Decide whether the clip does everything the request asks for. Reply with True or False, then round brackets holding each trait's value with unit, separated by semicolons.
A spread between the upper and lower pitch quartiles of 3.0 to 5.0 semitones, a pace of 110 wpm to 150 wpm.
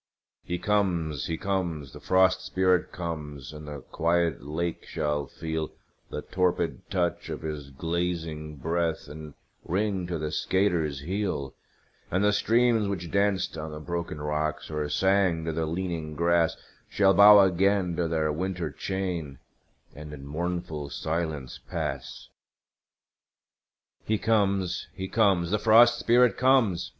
True (3.7 semitones; 140 wpm)